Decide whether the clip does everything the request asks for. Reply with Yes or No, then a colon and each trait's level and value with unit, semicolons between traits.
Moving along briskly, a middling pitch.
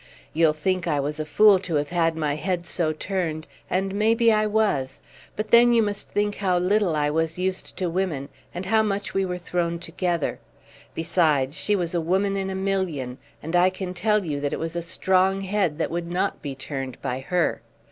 Yes: fast, 210 wpm; medium, 180 Hz